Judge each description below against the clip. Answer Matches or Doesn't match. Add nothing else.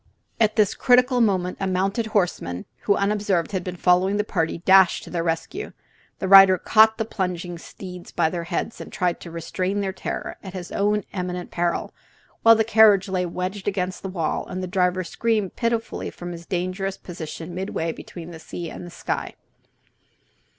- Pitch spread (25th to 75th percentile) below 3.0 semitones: Matches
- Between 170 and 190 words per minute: Matches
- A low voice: Doesn't match